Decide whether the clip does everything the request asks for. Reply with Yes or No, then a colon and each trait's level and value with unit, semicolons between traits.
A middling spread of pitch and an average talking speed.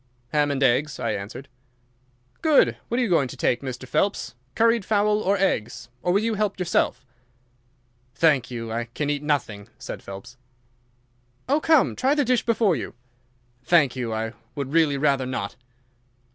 No: wide, 8.3 semitones; average, 160 wpm